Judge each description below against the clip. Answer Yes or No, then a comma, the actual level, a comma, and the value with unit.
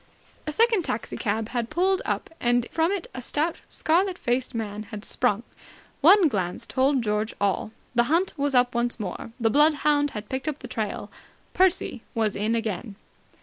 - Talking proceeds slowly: No, average, 180 wpm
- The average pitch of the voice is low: No, very high, 250 Hz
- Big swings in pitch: Yes, wide, 5.7 semitones